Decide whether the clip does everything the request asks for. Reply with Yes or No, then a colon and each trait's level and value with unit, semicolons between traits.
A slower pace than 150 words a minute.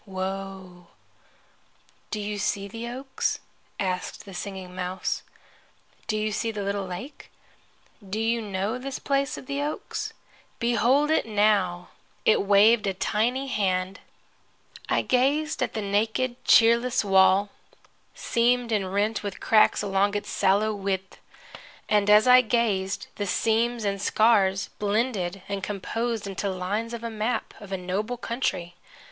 Yes: average, 140 wpm